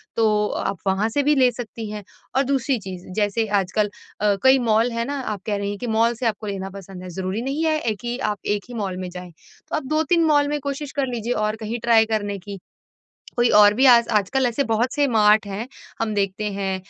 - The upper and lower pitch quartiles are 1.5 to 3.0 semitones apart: No, average, 3.9 semitones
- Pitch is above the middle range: Yes, high, 220 Hz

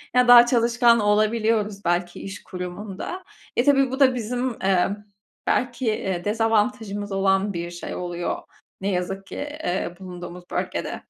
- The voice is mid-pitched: No, high, 210 Hz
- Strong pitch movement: No, average, 4.4 semitones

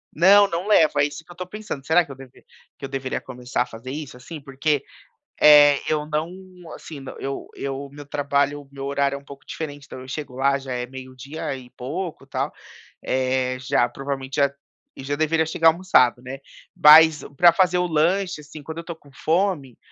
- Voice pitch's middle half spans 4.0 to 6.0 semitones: No, average, 3.1 semitones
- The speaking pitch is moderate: Yes, medium, 145 Hz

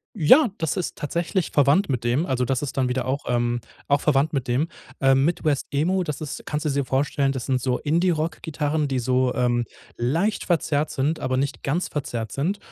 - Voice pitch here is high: No, medium, 140 Hz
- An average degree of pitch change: Yes, average, 3.5 semitones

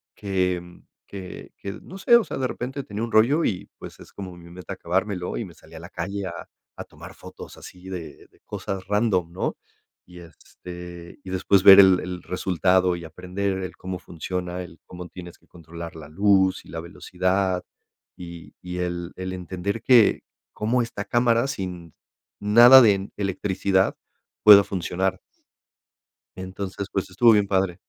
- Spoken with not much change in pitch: Yes, narrow, 2.2 semitones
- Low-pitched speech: Yes, very low, 95 Hz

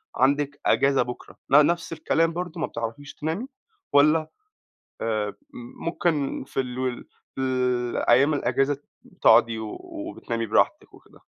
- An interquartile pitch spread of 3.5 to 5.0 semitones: Yes, average, 4.4 semitones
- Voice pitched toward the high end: No, medium, 140 Hz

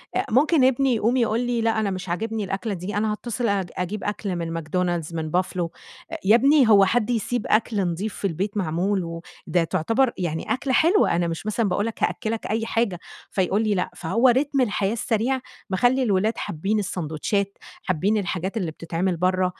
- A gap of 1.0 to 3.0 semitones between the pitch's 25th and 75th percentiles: No, average, 4.1 semitones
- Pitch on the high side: Yes, high, 205 Hz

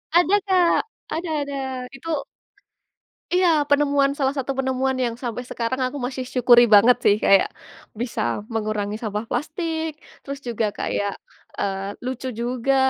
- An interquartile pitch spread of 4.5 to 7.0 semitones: No, average, 3.7 semitones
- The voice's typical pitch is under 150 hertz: No, very high, 255 Hz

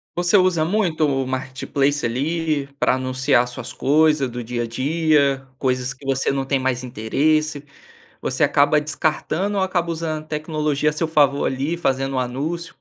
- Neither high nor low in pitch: Yes, medium, 145 Hz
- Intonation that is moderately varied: Yes, average, 3.2 semitones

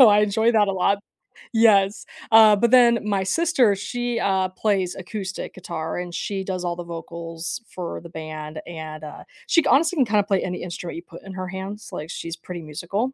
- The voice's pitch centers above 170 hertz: Yes, high, 190 Hz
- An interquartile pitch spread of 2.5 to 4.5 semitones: Yes, average, 4.1 semitones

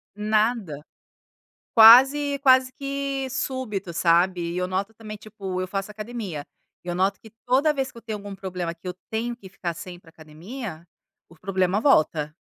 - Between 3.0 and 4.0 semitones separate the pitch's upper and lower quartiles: No, average, 5.1 semitones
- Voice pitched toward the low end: No, high, 205 Hz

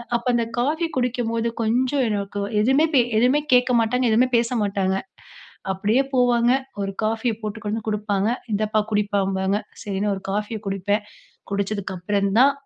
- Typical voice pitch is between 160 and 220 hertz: Yes, high, 215 Hz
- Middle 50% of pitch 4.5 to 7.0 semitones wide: No, average, 3.3 semitones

